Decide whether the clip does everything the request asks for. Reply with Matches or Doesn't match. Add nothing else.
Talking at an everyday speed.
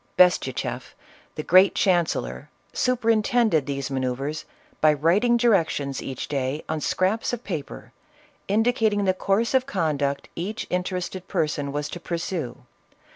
Doesn't match